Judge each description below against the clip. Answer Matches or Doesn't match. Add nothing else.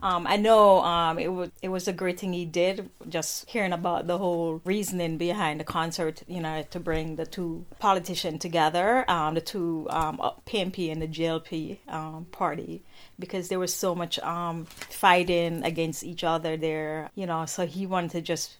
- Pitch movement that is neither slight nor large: Doesn't match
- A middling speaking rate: Matches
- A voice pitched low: Doesn't match